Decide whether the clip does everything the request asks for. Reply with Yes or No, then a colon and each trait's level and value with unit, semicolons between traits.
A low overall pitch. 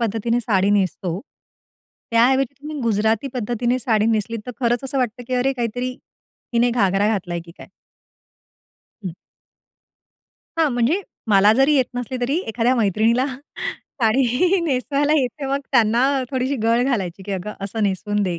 No: high, 235 Hz